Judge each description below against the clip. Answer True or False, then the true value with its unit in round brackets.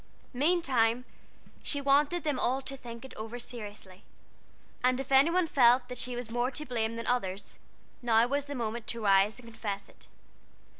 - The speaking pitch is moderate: False (245 Hz)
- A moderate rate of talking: True (185 wpm)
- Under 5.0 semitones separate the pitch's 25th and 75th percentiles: True (3.3 semitones)